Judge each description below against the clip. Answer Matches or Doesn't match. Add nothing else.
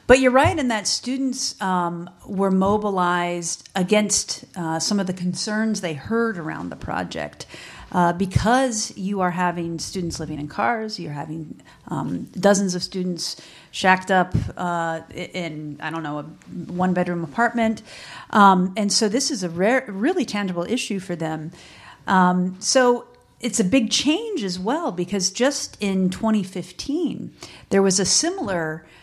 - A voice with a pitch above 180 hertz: Matches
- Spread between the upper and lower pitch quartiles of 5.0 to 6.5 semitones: Doesn't match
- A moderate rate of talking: Matches